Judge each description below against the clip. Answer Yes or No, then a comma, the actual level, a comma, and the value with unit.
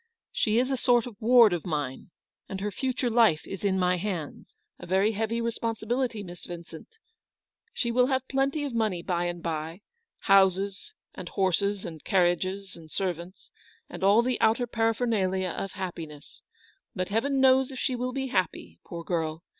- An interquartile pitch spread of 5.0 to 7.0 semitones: Yes, average, 5.3 semitones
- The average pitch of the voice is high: Yes, high, 200 Hz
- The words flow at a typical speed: Yes, average, 170 wpm